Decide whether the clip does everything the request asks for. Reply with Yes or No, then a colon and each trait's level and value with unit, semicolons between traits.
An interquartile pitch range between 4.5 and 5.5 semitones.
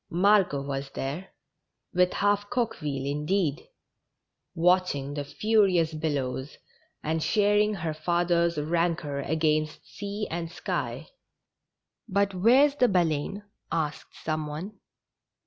Yes: average, 4.9 semitones